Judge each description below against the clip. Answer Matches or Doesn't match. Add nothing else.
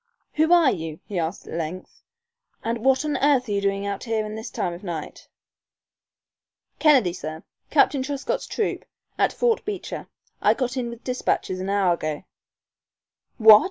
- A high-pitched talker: Matches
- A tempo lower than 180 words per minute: Matches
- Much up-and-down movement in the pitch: Matches